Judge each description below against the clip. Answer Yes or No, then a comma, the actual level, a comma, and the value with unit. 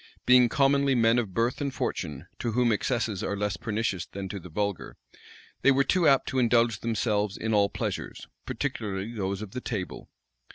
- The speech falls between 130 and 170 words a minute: No, average, 180 wpm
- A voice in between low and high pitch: No, low, 110 Hz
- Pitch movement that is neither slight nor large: Yes, average, 3.6 semitones